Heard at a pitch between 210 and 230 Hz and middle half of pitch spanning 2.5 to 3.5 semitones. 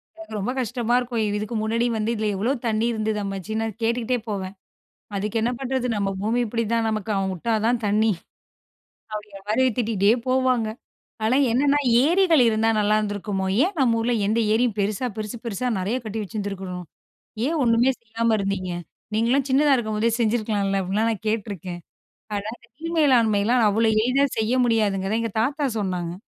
Yes: high, 220 Hz; average, 2.9 semitones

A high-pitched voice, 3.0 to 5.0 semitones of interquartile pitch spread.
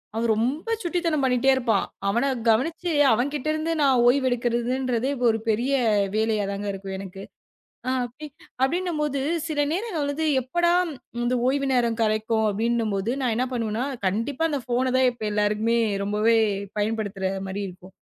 Yes: high, 240 Hz; average, 4.3 semitones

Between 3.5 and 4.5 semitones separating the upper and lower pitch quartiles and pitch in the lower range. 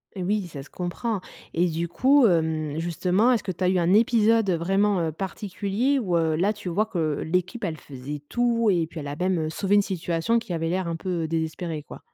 No: average, 4.1 semitones; medium, 180 Hz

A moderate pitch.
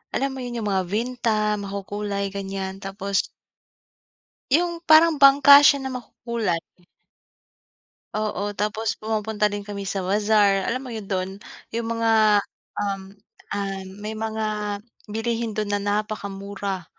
No: high, 210 Hz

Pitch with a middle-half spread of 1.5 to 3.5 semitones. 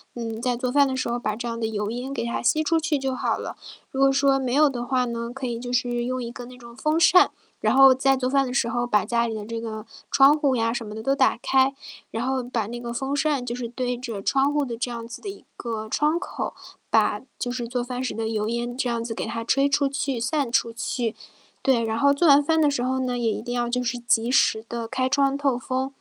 Yes: narrow, 2.5 semitones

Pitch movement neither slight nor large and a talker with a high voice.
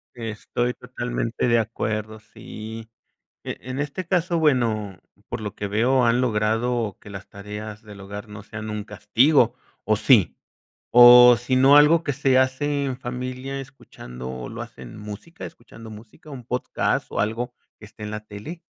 No: average, 3.4 semitones; low, 115 Hz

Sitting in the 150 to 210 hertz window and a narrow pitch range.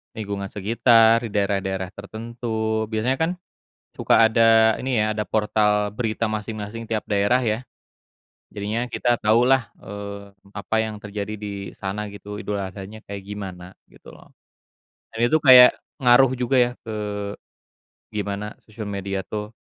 No: low, 110 Hz; narrow, 2.1 semitones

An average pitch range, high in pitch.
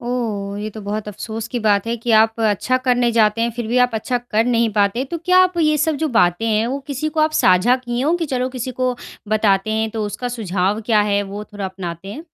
Yes: average, 3.4 semitones; high, 225 Hz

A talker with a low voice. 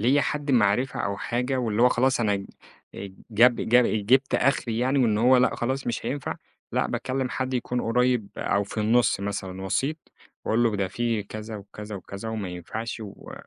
Yes: low, 115 Hz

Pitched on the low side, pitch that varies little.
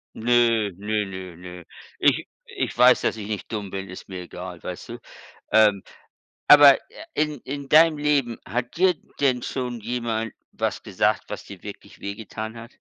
No: low, 115 Hz; average, 4.3 semitones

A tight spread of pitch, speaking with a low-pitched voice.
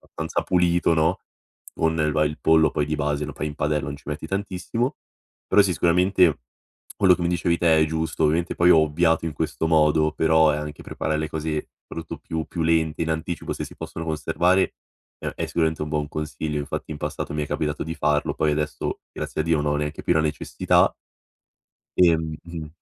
Yes: narrow, 1.6 semitones; very low, 80 Hz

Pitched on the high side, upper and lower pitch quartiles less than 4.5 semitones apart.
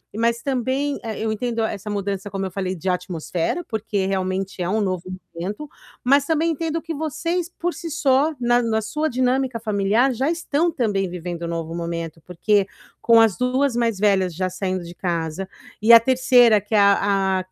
No: high, 215 Hz; wide, 5.5 semitones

